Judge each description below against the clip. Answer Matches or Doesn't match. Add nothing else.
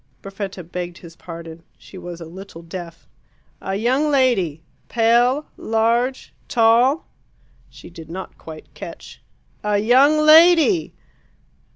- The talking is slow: Matches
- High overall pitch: Matches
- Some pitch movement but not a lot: Doesn't match